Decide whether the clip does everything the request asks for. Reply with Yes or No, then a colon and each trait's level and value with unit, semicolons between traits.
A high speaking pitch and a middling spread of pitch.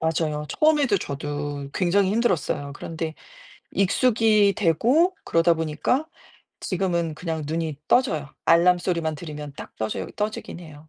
No: medium, 165 Hz; average, 4.8 semitones